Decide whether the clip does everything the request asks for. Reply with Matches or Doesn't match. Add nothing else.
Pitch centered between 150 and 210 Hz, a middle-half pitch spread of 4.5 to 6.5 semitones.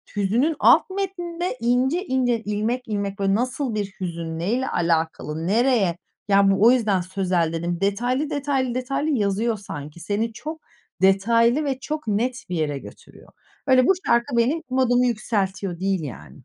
Doesn't match